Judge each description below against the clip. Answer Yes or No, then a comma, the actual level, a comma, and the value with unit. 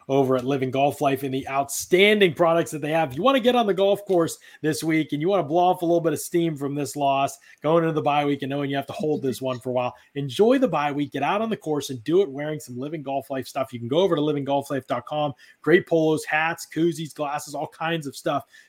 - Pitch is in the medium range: Yes, medium, 150 Hz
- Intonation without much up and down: No, average, 3.3 semitones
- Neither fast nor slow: No, fast, 275 wpm